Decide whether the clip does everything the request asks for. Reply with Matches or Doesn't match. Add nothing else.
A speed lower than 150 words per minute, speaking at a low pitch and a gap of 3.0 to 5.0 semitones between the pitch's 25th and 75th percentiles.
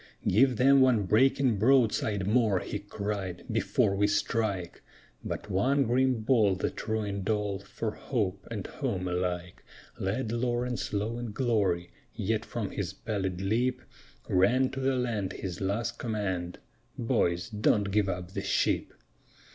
Matches